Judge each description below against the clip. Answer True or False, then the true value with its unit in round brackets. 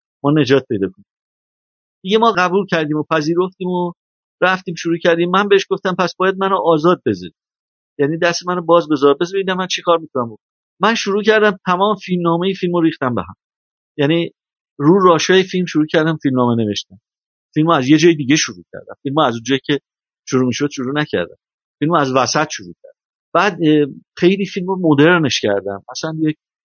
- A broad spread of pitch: False (4.2 semitones)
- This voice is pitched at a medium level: True (165 Hz)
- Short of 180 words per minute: False (185 wpm)